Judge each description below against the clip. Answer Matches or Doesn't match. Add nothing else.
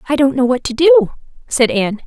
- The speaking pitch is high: Matches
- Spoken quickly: Matches